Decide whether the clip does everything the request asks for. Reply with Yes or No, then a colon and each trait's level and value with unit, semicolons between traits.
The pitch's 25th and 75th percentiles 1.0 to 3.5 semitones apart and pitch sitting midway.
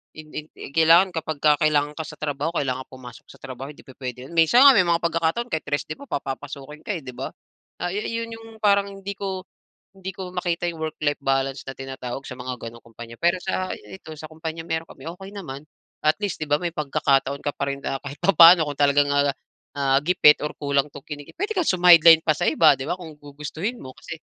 No: average, 4.2 semitones; medium, 155 Hz